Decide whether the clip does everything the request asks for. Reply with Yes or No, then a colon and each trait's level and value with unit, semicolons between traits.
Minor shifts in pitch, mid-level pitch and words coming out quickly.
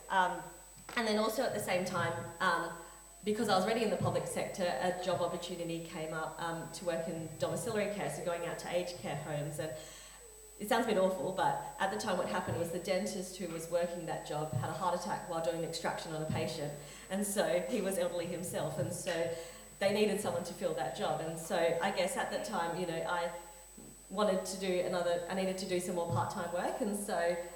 Yes: narrow, 2.0 semitones; medium, 175 Hz; fast, 225 wpm